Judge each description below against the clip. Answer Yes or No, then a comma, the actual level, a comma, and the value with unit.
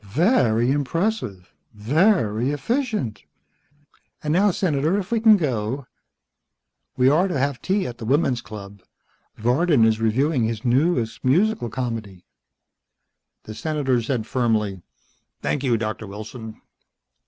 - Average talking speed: No, slow, 120 wpm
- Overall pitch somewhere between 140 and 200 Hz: No, low, 130 Hz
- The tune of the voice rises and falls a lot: Yes, wide, 6.5 semitones